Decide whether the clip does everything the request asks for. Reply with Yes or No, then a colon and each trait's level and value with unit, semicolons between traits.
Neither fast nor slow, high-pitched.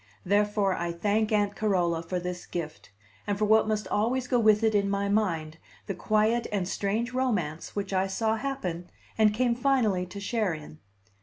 Yes: average, 180 wpm; high, 205 Hz